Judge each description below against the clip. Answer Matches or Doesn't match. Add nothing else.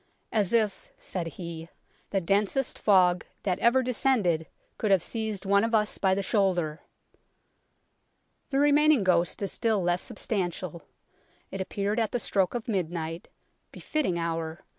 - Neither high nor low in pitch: Doesn't match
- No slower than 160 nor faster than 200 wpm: Doesn't match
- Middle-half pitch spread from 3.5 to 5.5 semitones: Matches